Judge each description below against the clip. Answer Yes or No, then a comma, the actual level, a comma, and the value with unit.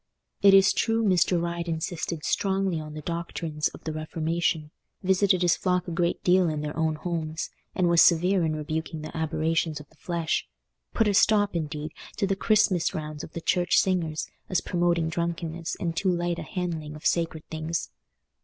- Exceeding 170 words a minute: Yes, average, 180 wpm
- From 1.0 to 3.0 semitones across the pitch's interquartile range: Yes, narrow, 2.4 semitones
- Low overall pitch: No, medium, 170 Hz